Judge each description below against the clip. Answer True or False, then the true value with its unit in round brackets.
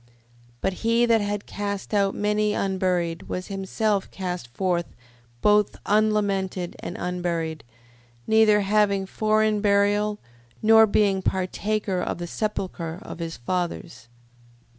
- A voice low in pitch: False (200 Hz)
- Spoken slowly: True (120 wpm)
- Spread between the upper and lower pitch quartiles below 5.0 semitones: True (2.8 semitones)